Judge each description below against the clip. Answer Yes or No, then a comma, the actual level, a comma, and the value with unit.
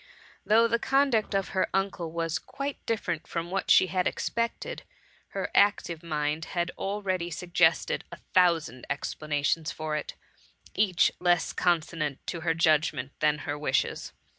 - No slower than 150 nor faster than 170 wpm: No, average, 140 wpm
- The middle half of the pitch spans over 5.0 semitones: No, average, 3.8 semitones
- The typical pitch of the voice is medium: Yes, medium, 170 Hz